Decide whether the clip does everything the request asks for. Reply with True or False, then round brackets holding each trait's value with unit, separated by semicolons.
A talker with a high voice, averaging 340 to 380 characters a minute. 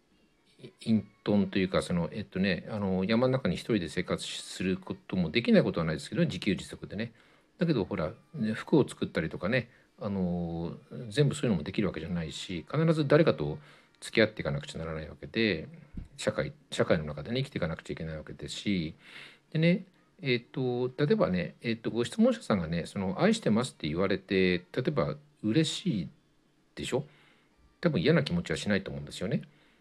False (120 Hz; 355 characters per minute)